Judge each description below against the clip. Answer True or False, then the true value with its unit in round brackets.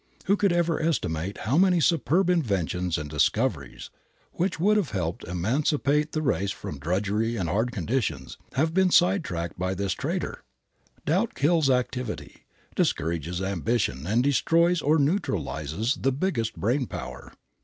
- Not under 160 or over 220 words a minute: False (145 wpm)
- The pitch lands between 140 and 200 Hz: False (120 Hz)